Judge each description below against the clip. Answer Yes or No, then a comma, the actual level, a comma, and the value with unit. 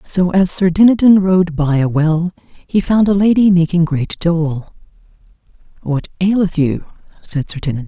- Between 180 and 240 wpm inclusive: No, average, 160 wpm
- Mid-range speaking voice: Yes, medium, 175 Hz